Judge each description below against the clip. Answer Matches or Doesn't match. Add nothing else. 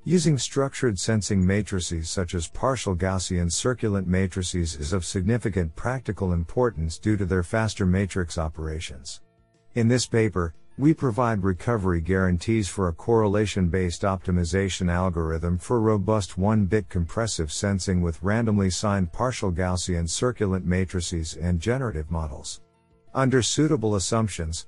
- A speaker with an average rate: Doesn't match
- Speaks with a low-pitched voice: Matches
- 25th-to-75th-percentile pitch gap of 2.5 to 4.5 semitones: Matches